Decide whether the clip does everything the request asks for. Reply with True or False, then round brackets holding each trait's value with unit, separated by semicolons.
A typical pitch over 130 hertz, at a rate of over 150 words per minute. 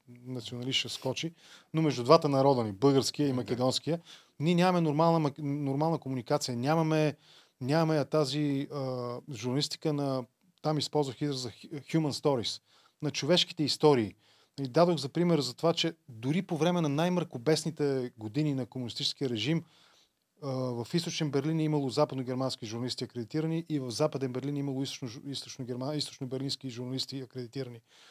False (140 Hz; 140 wpm)